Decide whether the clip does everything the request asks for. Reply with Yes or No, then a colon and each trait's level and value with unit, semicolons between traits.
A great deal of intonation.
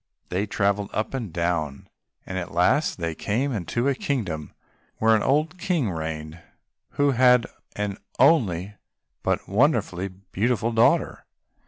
Yes: wide, 6.2 semitones